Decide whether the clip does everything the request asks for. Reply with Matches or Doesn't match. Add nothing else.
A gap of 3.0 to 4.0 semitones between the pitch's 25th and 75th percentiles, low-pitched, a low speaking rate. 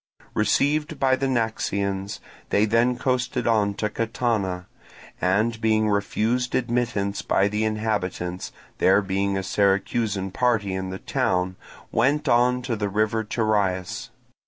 Matches